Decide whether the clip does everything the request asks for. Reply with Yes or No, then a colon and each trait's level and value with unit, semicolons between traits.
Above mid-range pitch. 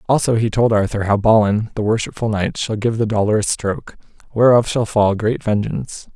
No: low, 110 Hz